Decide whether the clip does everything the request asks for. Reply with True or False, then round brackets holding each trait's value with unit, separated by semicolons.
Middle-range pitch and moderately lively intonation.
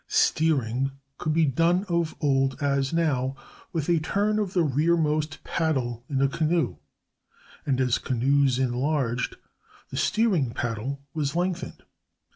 True (145 Hz; 3.9 semitones)